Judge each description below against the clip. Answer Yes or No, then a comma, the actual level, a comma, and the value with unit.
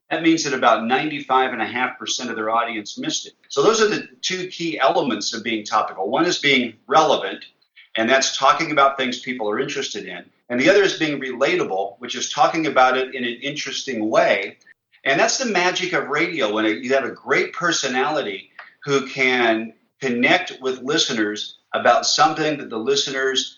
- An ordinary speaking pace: Yes, average, 180 wpm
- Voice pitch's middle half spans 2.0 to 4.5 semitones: No, average, 5.0 semitones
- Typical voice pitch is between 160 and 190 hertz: No, low, 135 Hz